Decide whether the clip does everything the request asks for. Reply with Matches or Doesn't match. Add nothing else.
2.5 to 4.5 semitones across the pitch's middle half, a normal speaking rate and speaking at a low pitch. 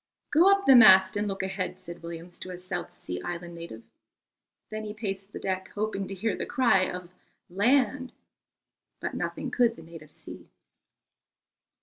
Doesn't match